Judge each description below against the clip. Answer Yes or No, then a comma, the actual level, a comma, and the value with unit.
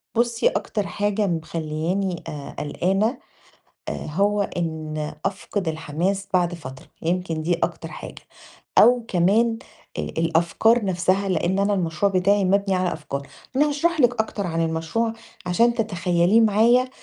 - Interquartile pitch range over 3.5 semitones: Yes, average, 4.3 semitones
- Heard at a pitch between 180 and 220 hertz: Yes, high, 190 Hz